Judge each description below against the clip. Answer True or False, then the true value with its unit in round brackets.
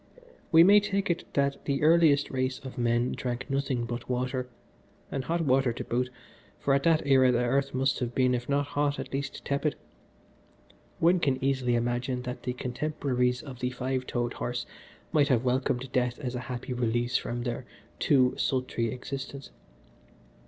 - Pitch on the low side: True (130 Hz)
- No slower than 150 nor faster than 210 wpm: True (175 wpm)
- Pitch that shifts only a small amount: True (2.1 semitones)